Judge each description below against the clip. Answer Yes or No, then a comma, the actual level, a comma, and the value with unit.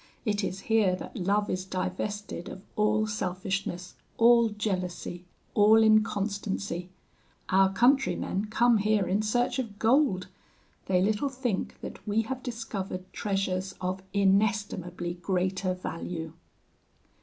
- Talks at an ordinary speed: No, slow, 120 wpm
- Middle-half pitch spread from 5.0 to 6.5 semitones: No, average, 2.8 semitones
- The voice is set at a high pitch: Yes, high, 200 Hz